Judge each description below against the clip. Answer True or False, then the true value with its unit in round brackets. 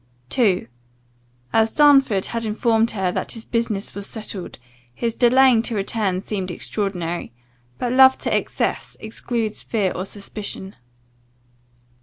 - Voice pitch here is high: True (220 Hz)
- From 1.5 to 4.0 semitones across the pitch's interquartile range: True (3.2 semitones)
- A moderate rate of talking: False (125 wpm)